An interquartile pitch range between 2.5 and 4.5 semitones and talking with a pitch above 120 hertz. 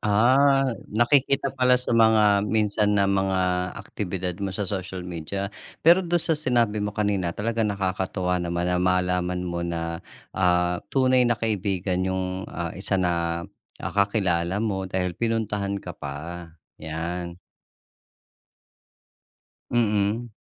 No: average, 3.5 semitones; very low, 95 Hz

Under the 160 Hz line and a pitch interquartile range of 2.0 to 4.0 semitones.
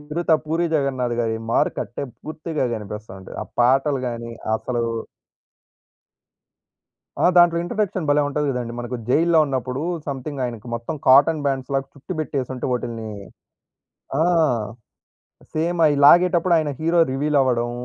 No: medium, 140 Hz; average, 4.4 semitones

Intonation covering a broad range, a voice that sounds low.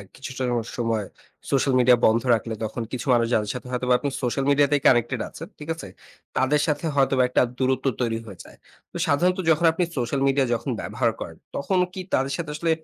No: average, 3.2 semitones; low, 130 Hz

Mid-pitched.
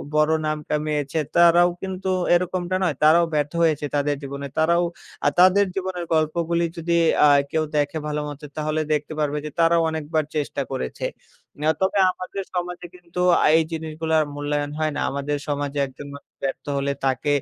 Yes: medium, 155 Hz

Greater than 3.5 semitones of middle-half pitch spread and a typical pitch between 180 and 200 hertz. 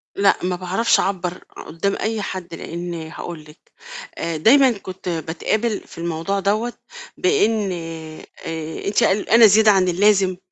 Yes: average, 3.9 semitones; high, 190 Hz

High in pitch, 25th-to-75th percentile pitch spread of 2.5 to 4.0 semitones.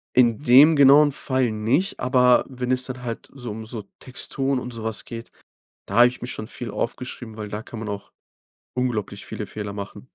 No: low, 125 Hz; average, 2.9 semitones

